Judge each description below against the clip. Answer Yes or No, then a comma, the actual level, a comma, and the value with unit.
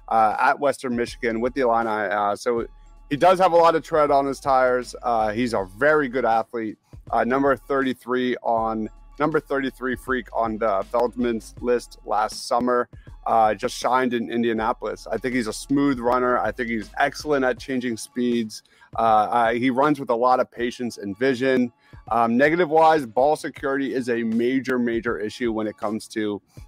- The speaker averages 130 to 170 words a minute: No, average, 180 wpm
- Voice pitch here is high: No, low, 120 Hz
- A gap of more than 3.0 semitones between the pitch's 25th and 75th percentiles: No, average, 2.7 semitones